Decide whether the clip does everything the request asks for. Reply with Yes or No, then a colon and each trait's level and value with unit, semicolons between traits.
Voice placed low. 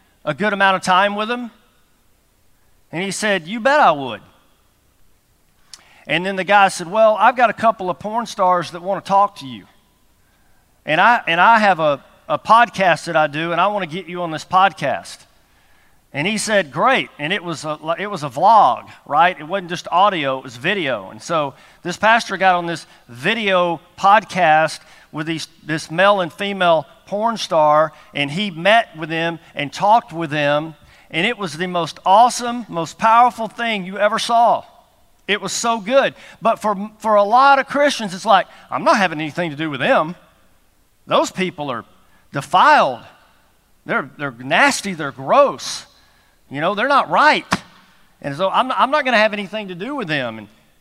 No: medium, 185 Hz